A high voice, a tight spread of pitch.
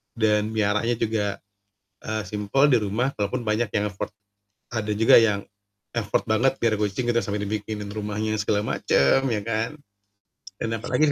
No: low, 110 Hz; narrow, 1.9 semitones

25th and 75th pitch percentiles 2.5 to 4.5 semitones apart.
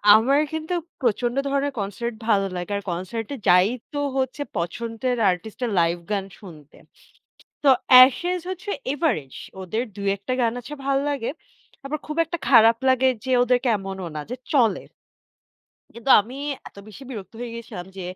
No: wide, 5.5 semitones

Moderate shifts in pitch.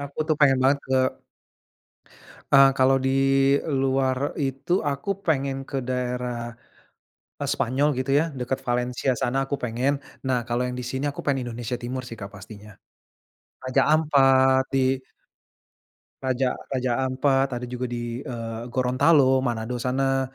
No: narrow, 1.7 semitones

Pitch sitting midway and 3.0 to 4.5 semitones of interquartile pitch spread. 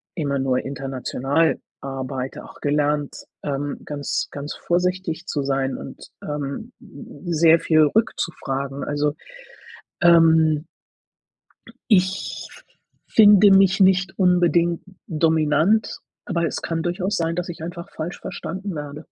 Yes: medium, 160 Hz; average, 3.8 semitones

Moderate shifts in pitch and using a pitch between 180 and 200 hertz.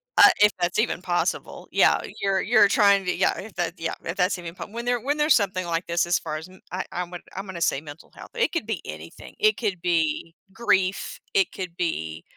Yes: average, 3.6 semitones; medium, 185 Hz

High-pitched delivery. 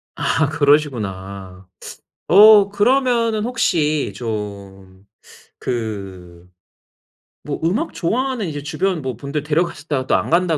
No: medium, 145 Hz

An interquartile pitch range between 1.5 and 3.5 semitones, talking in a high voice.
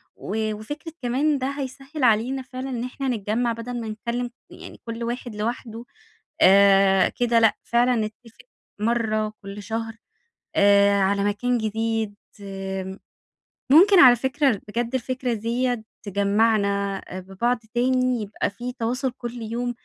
Yes: average, 3.2 semitones; high, 230 Hz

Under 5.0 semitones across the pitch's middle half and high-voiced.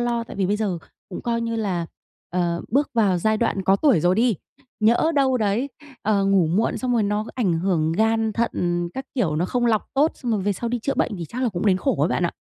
Yes: average, 4.3 semitones; high, 215 Hz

